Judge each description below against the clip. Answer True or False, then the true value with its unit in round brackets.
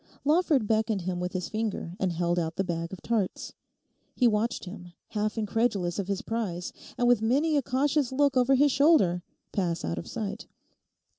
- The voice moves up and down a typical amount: False (5.9 semitones)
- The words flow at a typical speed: True (180 wpm)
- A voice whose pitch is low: False (215 Hz)